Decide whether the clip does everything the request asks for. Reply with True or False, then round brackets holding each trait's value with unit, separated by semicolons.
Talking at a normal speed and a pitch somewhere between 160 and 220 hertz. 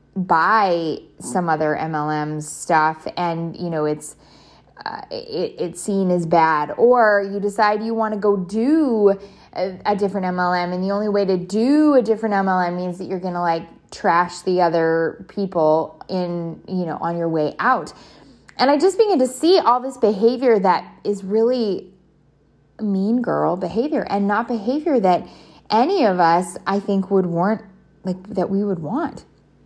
True (170 wpm; 190 Hz)